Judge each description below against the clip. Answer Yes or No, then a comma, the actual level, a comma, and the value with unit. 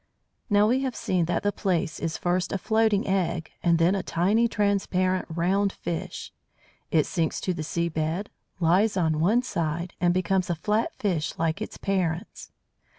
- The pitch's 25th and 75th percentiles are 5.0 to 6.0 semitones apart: No, average, 3.3 semitones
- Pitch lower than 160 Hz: No, medium, 180 Hz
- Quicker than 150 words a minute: Yes, average, 170 wpm